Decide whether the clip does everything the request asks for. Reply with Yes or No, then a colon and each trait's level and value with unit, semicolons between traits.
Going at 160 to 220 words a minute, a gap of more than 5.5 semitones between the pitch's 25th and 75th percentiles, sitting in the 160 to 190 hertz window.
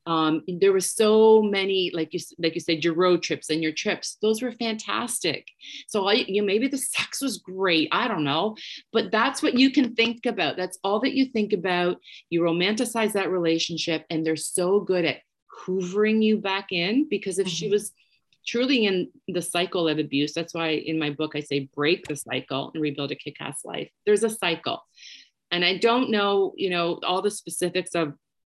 No: average, 200 wpm; average, 4.7 semitones; medium, 185 Hz